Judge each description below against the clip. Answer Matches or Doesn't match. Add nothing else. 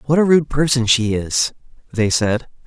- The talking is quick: Doesn't match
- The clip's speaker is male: Matches